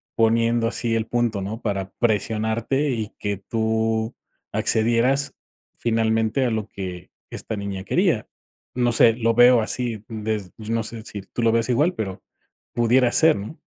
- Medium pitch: No, low, 115 Hz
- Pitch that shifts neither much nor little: No, narrow, 1.7 semitones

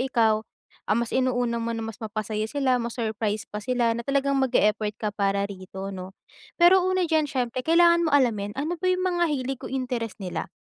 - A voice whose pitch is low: No, high, 240 Hz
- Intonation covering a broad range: No, average, 4.6 semitones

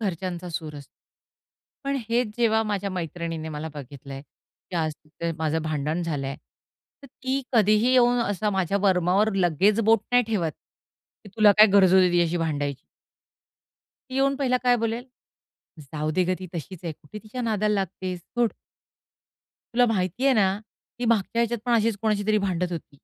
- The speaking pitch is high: Yes, high, 195 Hz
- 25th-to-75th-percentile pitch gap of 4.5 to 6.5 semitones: Yes, wide, 5.4 semitones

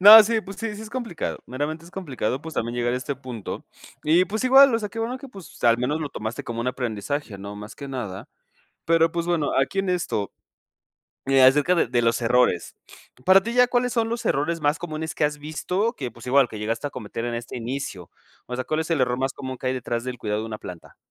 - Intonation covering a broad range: Yes, wide, 7.0 semitones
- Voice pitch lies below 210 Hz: Yes, medium, 140 Hz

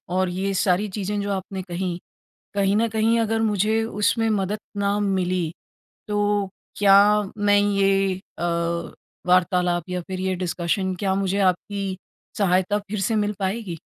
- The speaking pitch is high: Yes, high, 195 Hz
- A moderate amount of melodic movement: No, narrow, 2.1 semitones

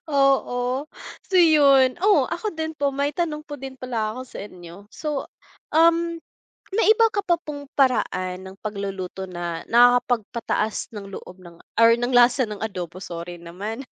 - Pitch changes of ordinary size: No, wide, 6.8 semitones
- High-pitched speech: Yes, high, 245 Hz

